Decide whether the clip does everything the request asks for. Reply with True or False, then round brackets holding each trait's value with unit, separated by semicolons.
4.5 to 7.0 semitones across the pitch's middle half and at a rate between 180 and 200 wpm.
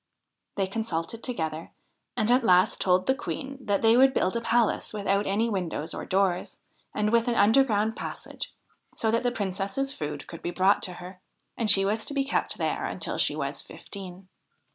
False (3.9 semitones; 185 wpm)